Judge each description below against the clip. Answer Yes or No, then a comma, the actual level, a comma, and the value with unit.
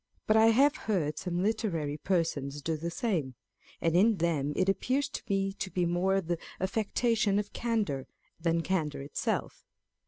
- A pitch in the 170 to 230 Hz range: Yes, medium, 185 Hz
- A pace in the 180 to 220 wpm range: No, average, 160 wpm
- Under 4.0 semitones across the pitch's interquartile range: No, average, 4.7 semitones